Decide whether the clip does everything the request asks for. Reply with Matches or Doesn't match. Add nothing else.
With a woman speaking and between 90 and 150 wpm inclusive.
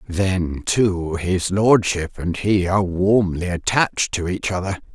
Matches